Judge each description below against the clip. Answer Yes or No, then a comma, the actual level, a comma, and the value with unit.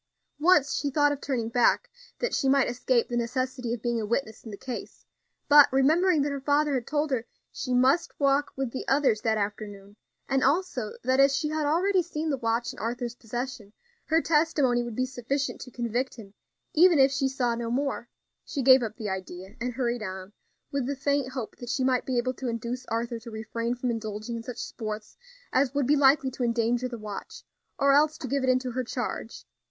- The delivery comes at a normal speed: No, fast, 210 wpm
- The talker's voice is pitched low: No, very high, 255 Hz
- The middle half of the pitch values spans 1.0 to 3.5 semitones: Yes, average, 3.2 semitones